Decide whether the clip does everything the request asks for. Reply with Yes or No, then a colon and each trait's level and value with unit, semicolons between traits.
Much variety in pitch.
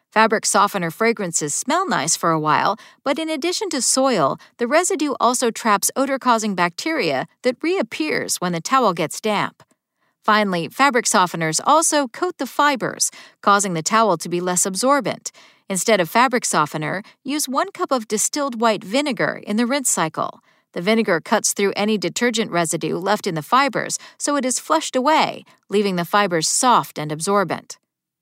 Yes: wide, 6.9 semitones